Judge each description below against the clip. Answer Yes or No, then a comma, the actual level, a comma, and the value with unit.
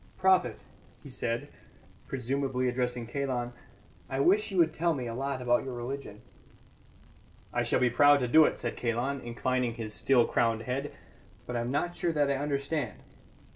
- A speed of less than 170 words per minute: No, average, 175 wpm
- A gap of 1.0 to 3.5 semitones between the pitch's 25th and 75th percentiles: Yes, average, 2.8 semitones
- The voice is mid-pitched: No, low, 130 Hz